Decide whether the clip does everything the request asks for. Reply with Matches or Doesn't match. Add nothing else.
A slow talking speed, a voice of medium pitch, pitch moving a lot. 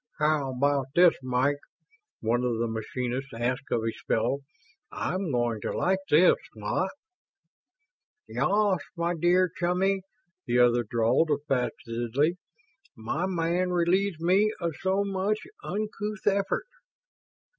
Matches